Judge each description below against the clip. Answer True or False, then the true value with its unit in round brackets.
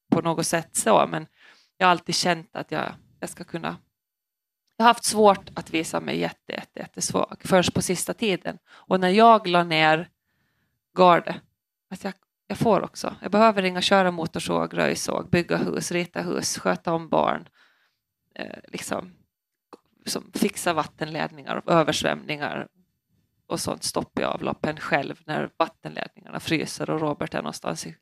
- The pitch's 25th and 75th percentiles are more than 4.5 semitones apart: False (3.1 semitones)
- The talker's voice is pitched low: False (175 Hz)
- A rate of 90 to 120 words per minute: False (155 wpm)